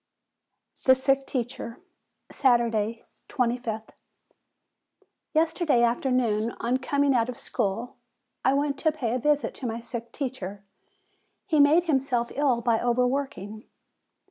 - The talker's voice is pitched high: Yes, very high, 250 Hz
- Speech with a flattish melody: No, average, 3.1 semitones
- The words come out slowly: Yes, slow, 120 wpm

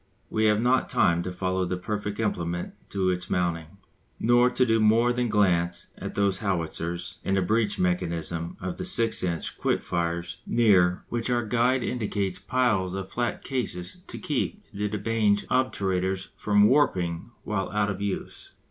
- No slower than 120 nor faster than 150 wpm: No, average, 165 wpm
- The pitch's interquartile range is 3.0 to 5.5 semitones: Yes, average, 4.1 semitones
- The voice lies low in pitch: Yes, low, 100 Hz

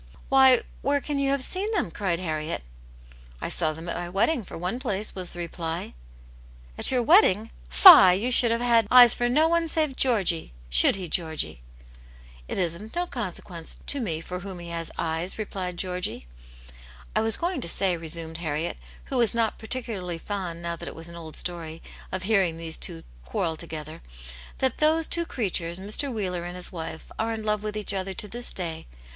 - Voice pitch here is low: No, medium, 185 Hz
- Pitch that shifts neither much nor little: No, wide, 6.1 semitones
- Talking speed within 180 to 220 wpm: Yes, average, 200 wpm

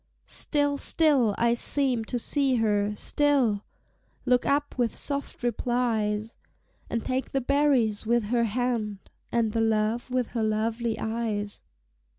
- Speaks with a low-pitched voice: No, high, 235 Hz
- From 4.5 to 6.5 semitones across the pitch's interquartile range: No, average, 2.9 semitones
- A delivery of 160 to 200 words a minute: No, slow, 135 wpm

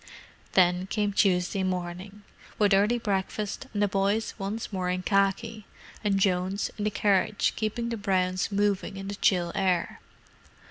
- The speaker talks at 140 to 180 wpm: Yes, average, 150 wpm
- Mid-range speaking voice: No, high, 195 Hz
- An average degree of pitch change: No, narrow, 1.9 semitones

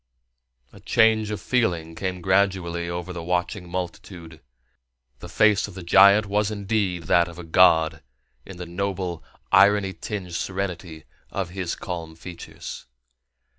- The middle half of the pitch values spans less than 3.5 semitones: Yes, narrow, 2.6 semitones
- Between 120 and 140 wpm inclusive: Yes, slow, 135 wpm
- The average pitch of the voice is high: No, very low, 90 Hz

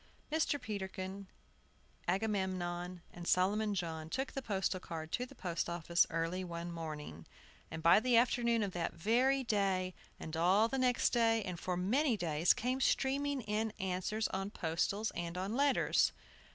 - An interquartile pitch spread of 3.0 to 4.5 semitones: No, average, 4.9 semitones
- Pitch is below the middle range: No, high, 190 Hz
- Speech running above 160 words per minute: No, average, 155 wpm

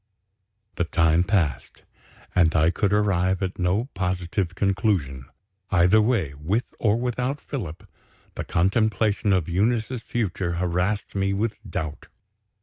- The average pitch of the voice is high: No, very low, 95 Hz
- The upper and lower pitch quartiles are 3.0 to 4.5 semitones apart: Yes, average, 3.7 semitones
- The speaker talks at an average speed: No, slow, 125 wpm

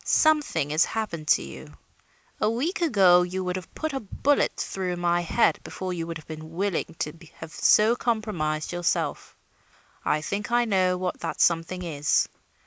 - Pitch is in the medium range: Yes, medium, 180 Hz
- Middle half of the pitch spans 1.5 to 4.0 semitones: No, average, 4.7 semitones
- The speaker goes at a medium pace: Yes, average, 170 wpm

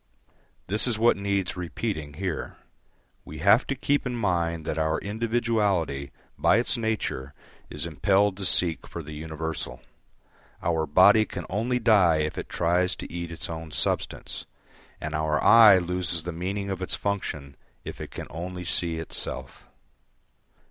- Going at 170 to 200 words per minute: No, average, 155 wpm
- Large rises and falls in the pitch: No, average, 4.2 semitones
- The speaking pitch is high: No, very low, 90 Hz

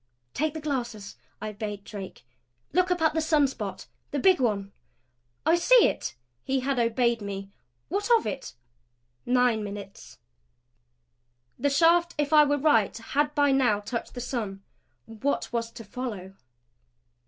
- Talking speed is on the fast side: No, average, 150 wpm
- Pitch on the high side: Yes, very high, 250 Hz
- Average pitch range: No, wide, 5.8 semitones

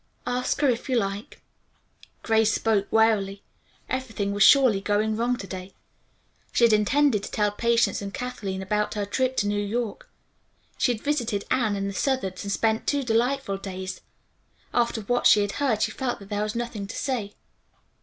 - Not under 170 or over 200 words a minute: Yes, average, 180 wpm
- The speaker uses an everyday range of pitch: Yes, average, 3.4 semitones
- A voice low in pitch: No, high, 220 Hz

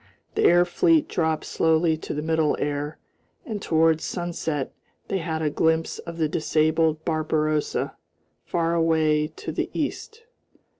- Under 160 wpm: Yes, average, 140 wpm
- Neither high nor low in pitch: Yes, medium, 160 Hz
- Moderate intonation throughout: No, narrow, 1.5 semitones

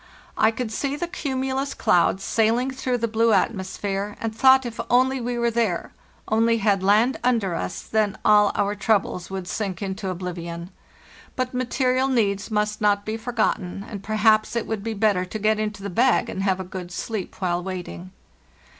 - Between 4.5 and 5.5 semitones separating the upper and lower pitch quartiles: No, average, 3.5 semitones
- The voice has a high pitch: Yes, high, 215 Hz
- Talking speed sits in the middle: Yes, average, 180 wpm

